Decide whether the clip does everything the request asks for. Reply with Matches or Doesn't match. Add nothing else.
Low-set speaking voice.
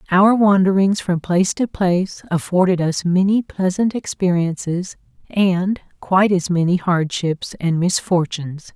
Doesn't match